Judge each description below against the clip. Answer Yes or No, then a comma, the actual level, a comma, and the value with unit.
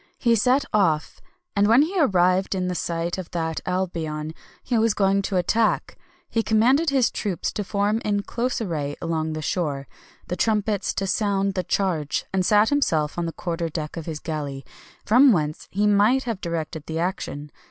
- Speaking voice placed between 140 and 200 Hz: Yes, high, 190 Hz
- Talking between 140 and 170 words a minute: No, average, 180 wpm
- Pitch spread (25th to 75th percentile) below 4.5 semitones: No, average, 4.9 semitones